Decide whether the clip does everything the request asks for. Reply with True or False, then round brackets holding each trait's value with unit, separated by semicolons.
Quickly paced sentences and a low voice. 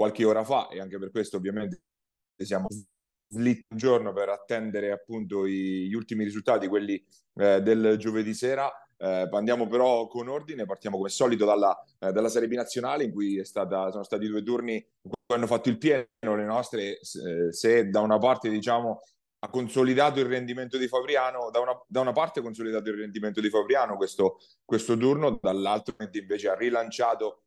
True (180 wpm; 110 Hz)